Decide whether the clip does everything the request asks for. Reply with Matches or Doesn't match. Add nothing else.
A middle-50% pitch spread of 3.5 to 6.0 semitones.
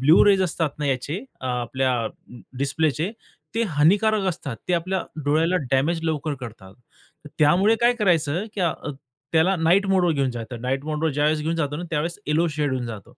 Matches